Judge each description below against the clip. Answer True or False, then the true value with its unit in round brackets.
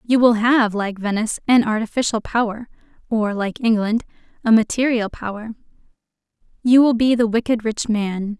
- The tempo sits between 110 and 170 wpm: True (150 wpm)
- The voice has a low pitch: False (225 Hz)